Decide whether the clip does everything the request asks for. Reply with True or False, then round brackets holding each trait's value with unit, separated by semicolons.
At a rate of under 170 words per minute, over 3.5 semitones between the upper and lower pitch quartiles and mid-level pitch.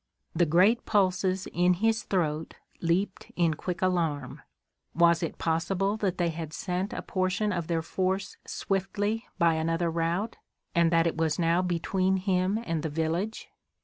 False (155 wpm; 2.5 semitones; 180 Hz)